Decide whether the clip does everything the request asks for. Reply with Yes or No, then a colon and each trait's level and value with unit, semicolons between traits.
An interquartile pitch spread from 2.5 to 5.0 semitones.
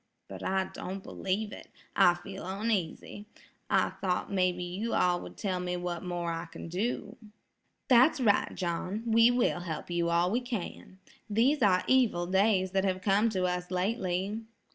Yes: average, 3.4 semitones